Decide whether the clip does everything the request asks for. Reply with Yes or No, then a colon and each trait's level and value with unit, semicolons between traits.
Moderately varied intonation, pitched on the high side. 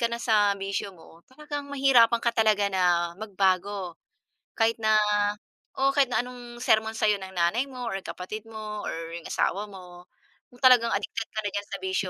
Yes: average, 3.9 semitones; high, 215 Hz